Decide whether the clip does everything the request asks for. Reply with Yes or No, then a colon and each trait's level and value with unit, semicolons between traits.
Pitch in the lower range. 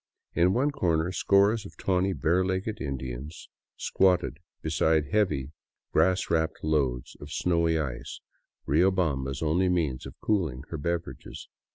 Yes: very low, 80 Hz